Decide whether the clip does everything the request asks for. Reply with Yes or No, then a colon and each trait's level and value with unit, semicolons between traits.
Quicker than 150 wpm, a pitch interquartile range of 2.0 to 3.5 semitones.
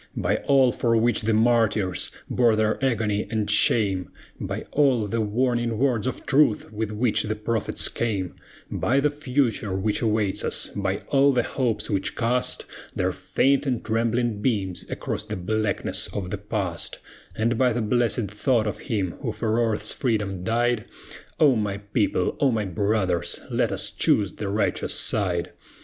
Yes: average, 165 wpm; average, 2.8 semitones